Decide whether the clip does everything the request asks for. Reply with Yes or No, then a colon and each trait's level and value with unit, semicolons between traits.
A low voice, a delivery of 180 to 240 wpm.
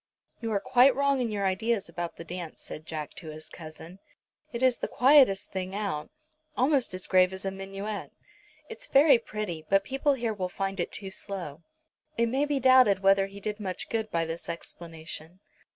No: high, 195 Hz; average, 190 wpm